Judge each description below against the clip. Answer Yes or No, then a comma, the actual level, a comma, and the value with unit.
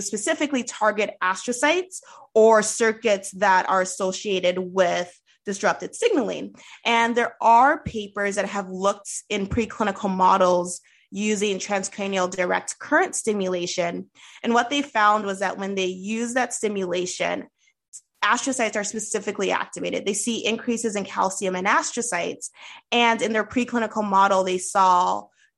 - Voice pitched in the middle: No, high, 210 Hz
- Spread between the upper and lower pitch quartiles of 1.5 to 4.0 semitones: Yes, average, 3.5 semitones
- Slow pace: Yes, slow, 130 wpm